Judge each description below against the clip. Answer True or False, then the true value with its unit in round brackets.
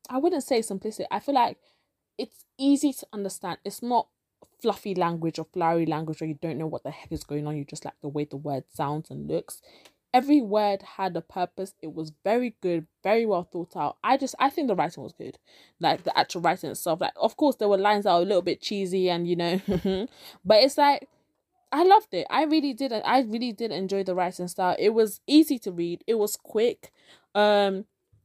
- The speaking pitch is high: True (195 Hz)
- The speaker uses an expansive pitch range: True (6.5 semitones)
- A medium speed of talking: False (220 wpm)